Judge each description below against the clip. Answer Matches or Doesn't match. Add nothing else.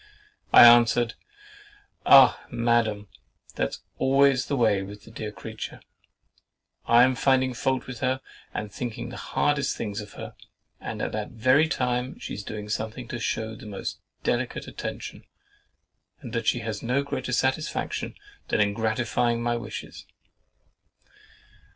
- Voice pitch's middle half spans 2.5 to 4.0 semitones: Matches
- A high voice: Doesn't match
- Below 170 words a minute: Matches